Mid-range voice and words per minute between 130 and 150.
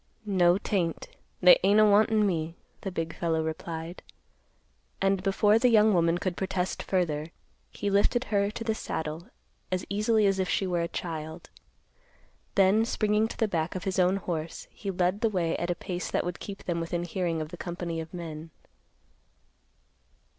No: medium, 180 Hz; average, 175 wpm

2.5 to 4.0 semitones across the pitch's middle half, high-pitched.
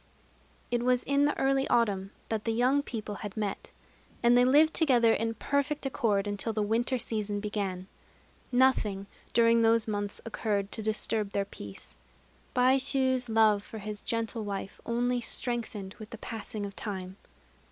Yes: average, 3.2 semitones; high, 225 Hz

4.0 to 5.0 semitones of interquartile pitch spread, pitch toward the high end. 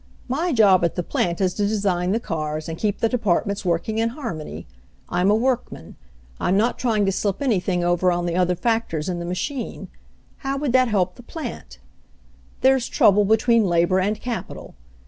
Yes: average, 4.7 semitones; high, 200 Hz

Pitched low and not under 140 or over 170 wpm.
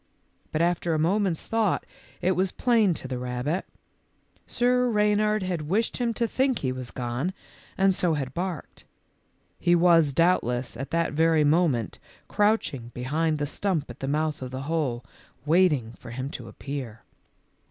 No: medium, 160 Hz; average, 165 wpm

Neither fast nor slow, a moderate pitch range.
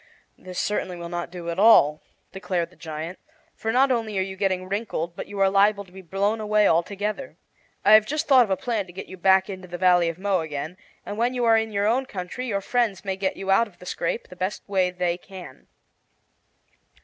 No: fast, 230 wpm; average, 3.0 semitones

